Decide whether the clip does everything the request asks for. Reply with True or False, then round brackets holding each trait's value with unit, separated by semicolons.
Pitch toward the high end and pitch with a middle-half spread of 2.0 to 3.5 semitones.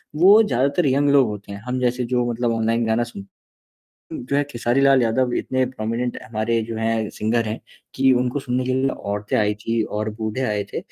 False (120 Hz; 2.7 semitones)